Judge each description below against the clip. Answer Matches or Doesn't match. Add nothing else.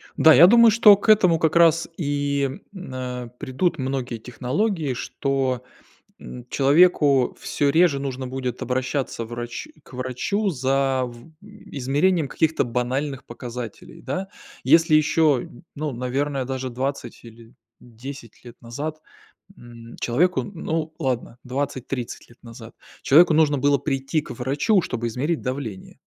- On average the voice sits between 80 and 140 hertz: Matches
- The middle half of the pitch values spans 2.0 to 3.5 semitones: Doesn't match